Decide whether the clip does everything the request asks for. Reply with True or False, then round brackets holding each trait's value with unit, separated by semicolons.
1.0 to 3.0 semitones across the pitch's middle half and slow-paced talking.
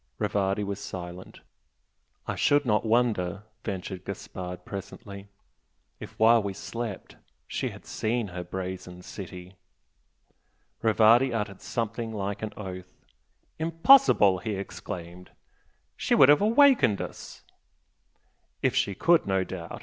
False (3.8 semitones; 120 wpm)